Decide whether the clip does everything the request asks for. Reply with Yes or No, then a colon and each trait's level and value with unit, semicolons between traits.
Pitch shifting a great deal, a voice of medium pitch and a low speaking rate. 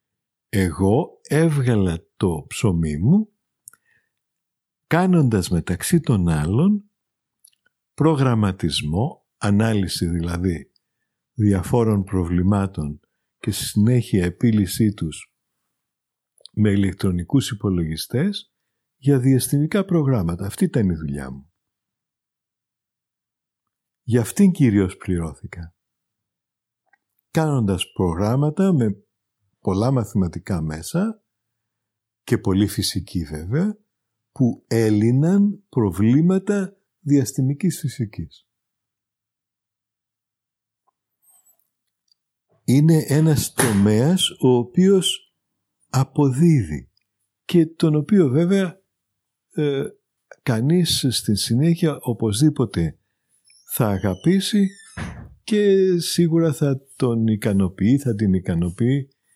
No: wide, 7.6 semitones; low, 115 Hz; slow, 75 wpm